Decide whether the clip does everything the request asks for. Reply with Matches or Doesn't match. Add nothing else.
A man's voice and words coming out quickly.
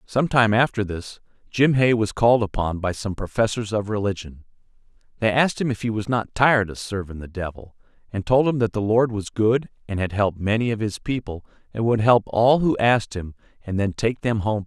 Matches